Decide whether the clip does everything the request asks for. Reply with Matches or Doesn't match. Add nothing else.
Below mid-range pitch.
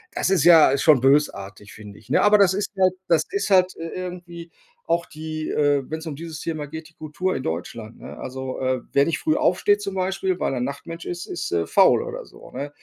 Doesn't match